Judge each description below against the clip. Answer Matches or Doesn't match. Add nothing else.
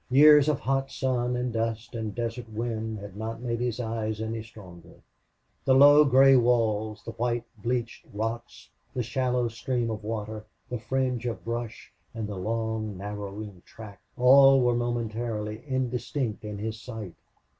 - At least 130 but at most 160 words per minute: Matches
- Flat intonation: Matches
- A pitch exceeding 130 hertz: Doesn't match